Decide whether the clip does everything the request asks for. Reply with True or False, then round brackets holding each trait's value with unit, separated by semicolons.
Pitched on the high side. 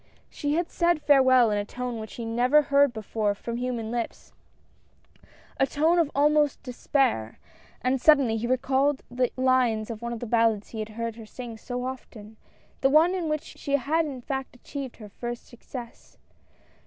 True (250 Hz)